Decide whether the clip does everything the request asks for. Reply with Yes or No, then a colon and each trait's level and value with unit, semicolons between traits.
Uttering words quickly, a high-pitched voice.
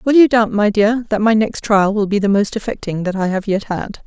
Yes: fast, 280 wpm; high, 210 Hz